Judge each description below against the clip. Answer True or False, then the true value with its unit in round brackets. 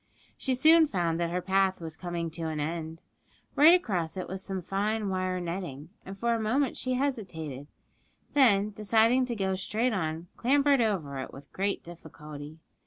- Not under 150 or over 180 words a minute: True (175 wpm)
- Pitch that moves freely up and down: True (5.7 semitones)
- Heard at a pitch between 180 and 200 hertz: True (190 Hz)